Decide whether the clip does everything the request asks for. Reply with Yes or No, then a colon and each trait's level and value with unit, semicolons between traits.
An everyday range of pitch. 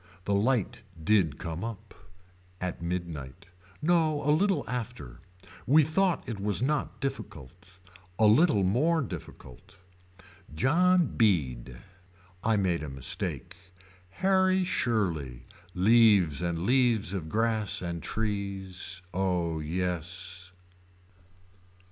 No: wide, 6.5 semitones